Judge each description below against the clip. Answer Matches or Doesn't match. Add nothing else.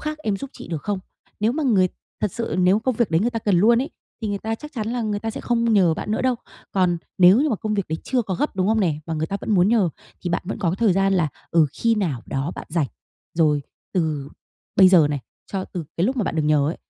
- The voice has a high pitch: Matches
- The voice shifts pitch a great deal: Doesn't match